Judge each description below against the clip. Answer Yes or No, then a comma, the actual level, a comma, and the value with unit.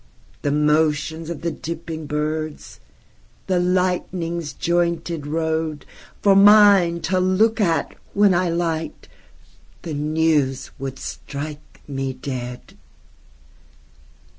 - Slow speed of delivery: Yes, slow, 90 wpm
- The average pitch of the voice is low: No, medium, 160 Hz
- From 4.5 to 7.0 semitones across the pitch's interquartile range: No, average, 3.0 semitones